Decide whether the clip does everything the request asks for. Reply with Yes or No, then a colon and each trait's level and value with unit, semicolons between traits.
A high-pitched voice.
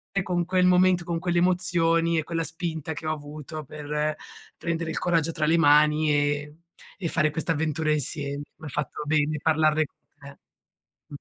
No: medium, 155 Hz